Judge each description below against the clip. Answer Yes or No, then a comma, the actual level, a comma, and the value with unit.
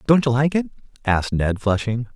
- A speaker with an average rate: Yes, average, 195 wpm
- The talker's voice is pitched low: Yes, low, 125 Hz